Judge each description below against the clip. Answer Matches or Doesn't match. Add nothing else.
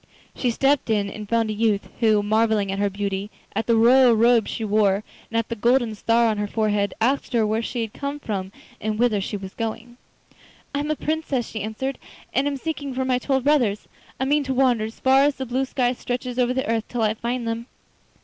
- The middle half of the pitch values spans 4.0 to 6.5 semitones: Doesn't match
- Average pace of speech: Doesn't match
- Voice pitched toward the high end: Matches